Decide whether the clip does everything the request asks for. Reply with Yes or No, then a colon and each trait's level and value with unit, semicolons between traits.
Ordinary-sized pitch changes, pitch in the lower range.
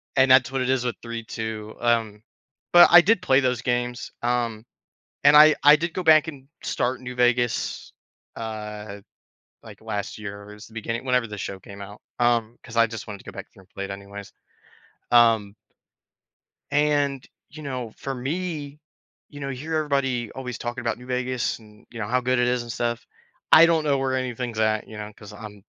Yes: average, 3.6 semitones; low, 120 Hz